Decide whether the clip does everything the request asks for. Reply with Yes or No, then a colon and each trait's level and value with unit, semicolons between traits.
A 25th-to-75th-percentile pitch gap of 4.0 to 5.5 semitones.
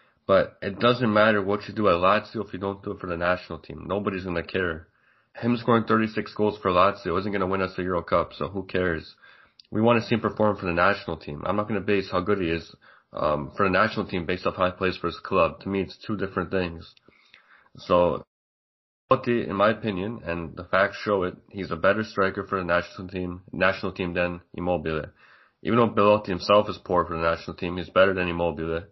No: average, 3.0 semitones